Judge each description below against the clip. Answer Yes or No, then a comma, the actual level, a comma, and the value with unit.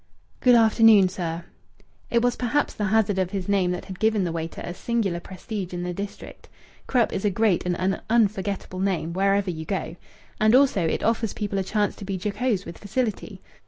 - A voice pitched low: No, high, 195 Hz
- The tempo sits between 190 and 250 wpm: Yes, average, 195 wpm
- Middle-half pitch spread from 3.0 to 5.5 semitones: Yes, average, 3.4 semitones